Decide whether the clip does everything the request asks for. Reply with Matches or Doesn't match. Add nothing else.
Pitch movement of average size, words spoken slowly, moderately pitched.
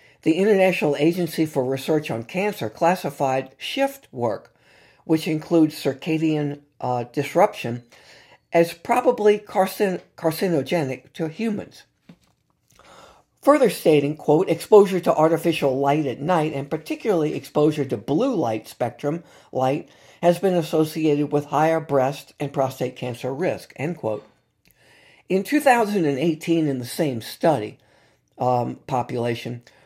Matches